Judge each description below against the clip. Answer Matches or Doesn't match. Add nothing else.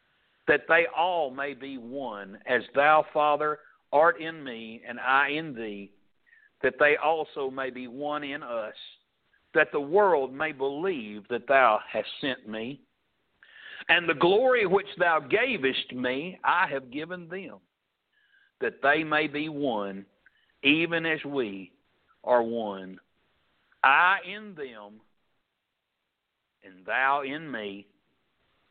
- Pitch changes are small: Doesn't match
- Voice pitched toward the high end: Doesn't match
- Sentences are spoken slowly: Matches